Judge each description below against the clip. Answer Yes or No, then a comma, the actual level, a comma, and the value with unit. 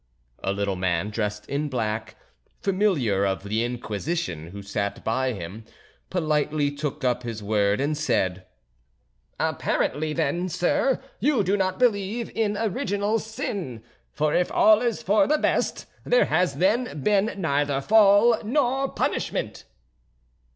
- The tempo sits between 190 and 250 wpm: No, slow, 135 wpm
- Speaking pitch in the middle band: Yes, medium, 150 Hz